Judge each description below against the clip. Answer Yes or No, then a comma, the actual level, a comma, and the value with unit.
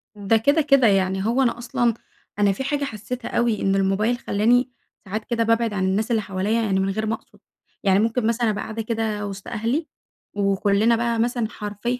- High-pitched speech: Yes, high, 220 Hz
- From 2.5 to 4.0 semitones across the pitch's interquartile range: Yes, average, 2.8 semitones